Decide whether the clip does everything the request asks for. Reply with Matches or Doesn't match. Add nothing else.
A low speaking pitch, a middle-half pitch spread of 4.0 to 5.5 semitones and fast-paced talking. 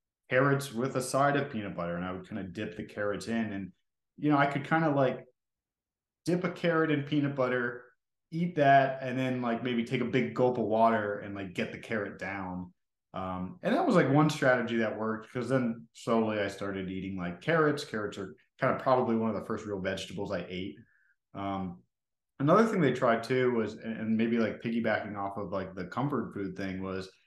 Matches